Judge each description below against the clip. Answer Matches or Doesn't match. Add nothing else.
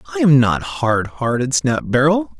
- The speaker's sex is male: Matches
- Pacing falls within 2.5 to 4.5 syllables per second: Matches